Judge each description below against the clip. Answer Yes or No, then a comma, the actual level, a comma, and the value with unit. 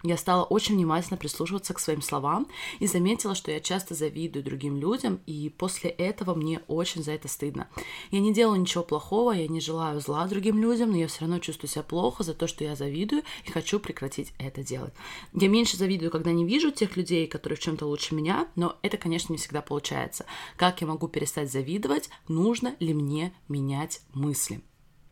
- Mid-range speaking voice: Yes, medium, 165 Hz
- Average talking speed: No, fast, 195 wpm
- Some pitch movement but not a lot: Yes, average, 4.1 semitones